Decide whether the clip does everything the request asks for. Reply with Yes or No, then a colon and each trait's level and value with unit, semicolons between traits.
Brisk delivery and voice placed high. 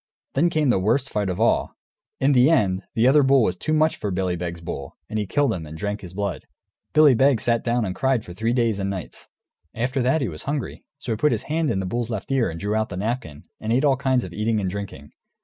No: fast, 265 wpm; low, 115 Hz